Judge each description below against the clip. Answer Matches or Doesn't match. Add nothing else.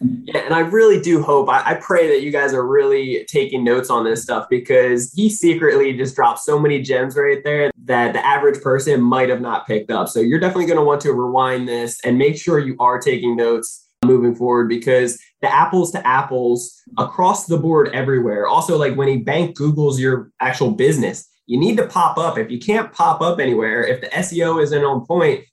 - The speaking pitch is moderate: Matches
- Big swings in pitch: Matches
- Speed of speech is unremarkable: Doesn't match